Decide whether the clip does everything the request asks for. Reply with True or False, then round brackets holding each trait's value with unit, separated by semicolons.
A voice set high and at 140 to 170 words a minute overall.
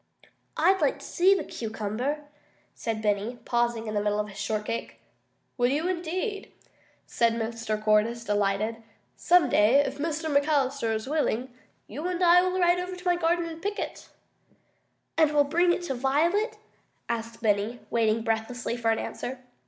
True (250 Hz; 165 wpm)